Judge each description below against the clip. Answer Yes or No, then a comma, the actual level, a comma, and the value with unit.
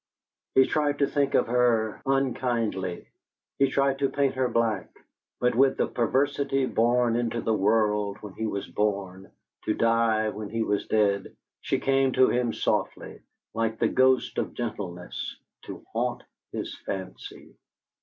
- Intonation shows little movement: No, average, 3.7 semitones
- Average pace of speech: Yes, average, 150 wpm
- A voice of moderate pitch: No, low, 115 Hz